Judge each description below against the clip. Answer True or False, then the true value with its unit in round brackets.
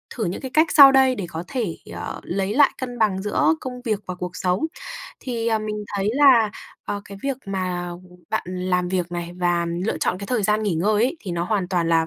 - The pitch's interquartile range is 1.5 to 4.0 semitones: False (4.7 semitones)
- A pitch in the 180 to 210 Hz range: True (200 Hz)